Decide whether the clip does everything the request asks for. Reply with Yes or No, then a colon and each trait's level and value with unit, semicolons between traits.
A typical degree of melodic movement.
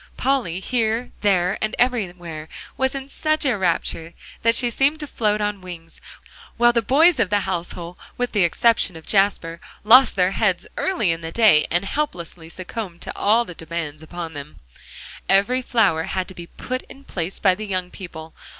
No: wide, 5.7 semitones